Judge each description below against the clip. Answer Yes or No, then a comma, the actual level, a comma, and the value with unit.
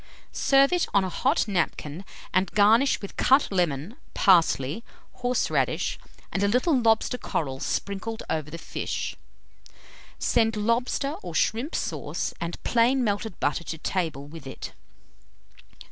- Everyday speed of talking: No, slow, 130 wpm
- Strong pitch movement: Yes, wide, 6.6 semitones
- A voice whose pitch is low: No, high, 205 Hz